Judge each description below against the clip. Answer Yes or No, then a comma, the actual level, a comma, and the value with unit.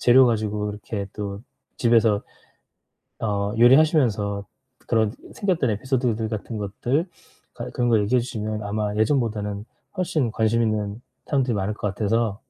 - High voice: No, low, 110 Hz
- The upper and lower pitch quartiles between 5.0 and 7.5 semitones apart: No, average, 2.7 semitones